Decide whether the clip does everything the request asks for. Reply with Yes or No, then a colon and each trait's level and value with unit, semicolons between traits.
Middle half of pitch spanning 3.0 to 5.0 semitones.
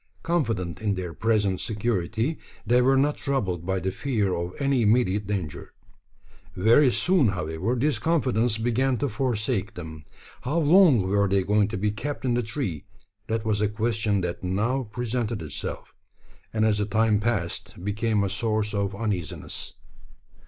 Yes: average, 3.9 semitones